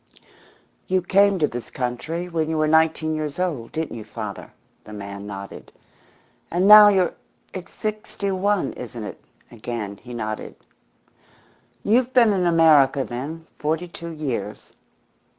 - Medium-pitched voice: Yes, medium, 160 Hz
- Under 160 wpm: Yes, average, 140 wpm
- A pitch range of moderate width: No, wide, 7.2 semitones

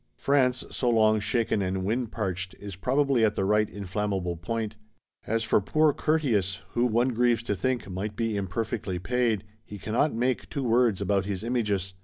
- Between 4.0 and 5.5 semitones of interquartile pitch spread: No, average, 3.5 semitones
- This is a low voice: Yes, low, 110 Hz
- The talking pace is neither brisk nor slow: Yes, average, 170 wpm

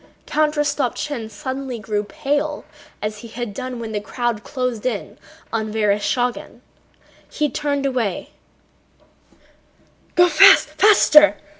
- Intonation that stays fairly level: No, average, 4.3 semitones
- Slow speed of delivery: Yes, slow, 100 wpm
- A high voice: Yes, high, 245 Hz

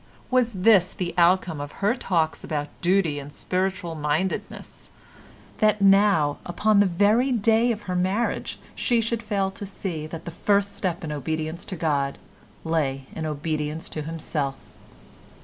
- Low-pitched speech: No, medium, 180 Hz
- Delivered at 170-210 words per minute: No, average, 150 wpm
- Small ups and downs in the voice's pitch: No, average, 4.5 semitones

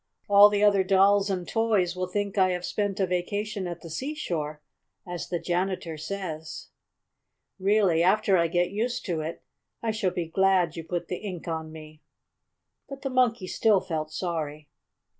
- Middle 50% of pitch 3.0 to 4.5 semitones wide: Yes, average, 3.4 semitones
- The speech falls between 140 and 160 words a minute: No, average, 170 wpm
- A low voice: No, medium, 185 Hz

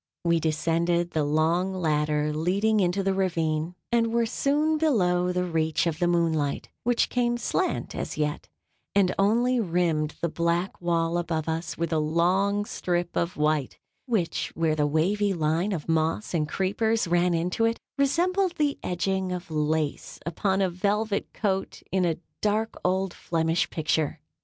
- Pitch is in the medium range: Yes, medium, 175 Hz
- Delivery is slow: No, average, 155 wpm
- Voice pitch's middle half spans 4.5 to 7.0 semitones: No, average, 3.9 semitones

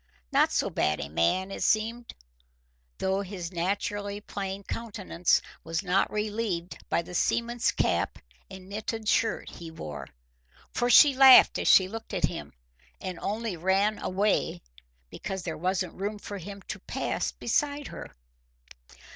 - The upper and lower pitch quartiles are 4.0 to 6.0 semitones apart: No, average, 3.2 semitones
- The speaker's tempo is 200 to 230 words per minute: No, average, 145 wpm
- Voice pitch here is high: Yes, high, 195 Hz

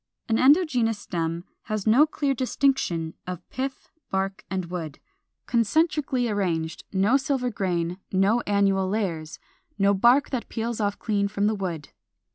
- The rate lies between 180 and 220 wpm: No, average, 140 wpm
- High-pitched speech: Yes, high, 205 Hz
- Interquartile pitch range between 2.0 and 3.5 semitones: No, average, 4.9 semitones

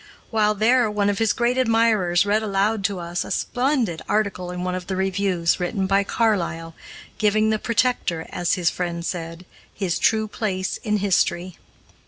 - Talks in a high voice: Yes, high, 200 Hz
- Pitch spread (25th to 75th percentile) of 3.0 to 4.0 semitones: Yes, average, 3.5 semitones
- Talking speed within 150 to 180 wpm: Yes, average, 170 wpm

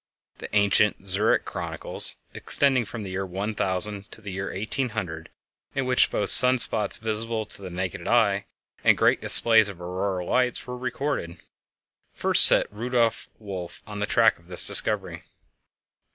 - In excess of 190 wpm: No, average, 155 wpm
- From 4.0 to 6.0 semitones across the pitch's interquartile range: No, average, 3.5 semitones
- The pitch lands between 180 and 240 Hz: No, low, 105 Hz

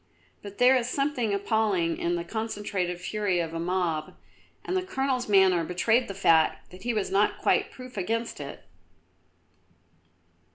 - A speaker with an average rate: Yes, average, 155 wpm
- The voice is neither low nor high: No, high, 200 Hz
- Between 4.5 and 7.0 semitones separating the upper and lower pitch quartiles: Yes, average, 5.0 semitones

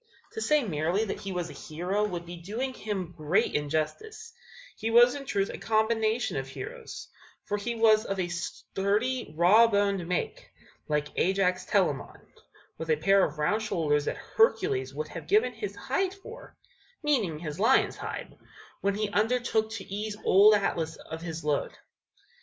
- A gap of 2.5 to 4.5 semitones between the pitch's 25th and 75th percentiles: No, average, 5.2 semitones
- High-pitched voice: Yes, high, 200 Hz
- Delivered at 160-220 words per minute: Yes, average, 165 wpm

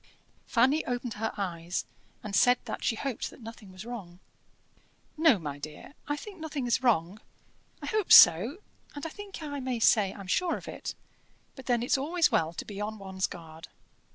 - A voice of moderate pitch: No, high, 235 Hz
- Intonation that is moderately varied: No, wide, 7.0 semitones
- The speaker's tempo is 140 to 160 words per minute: No, average, 185 wpm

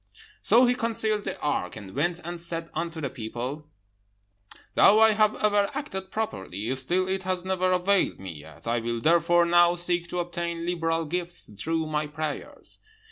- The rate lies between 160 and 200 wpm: Yes, average, 170 wpm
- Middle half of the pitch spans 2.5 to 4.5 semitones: Yes, average, 4.0 semitones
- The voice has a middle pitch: Yes, medium, 170 Hz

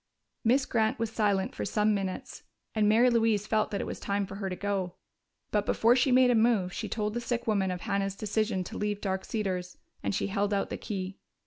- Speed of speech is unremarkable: No, fast, 225 wpm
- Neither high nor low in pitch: No, high, 210 Hz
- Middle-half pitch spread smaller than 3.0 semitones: Yes, narrow, 2.4 semitones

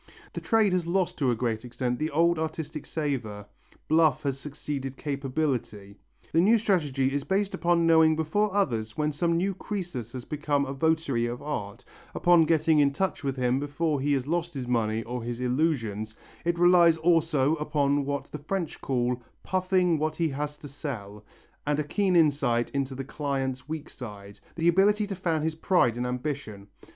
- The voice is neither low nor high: Yes, medium, 145 Hz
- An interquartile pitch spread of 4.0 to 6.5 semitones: Yes, average, 4.6 semitones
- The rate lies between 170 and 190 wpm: Yes, average, 180 wpm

